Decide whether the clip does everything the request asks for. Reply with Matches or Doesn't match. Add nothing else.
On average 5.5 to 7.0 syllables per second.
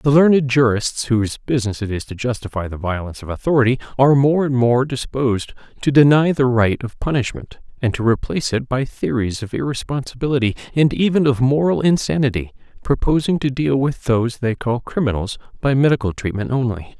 Matches